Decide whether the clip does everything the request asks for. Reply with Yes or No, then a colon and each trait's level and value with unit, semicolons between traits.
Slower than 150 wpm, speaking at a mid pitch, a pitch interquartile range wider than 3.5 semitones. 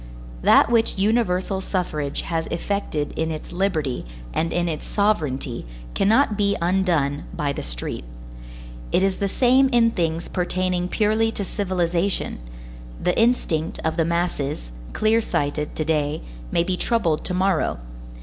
Yes: average, 140 wpm; medium, 180 Hz; average, 4.3 semitones